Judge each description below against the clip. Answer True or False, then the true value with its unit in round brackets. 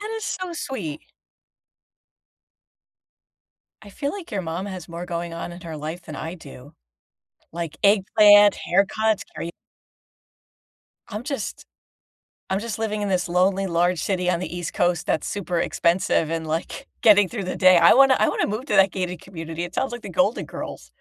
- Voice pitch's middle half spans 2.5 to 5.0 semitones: True (3.7 semitones)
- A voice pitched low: False (185 Hz)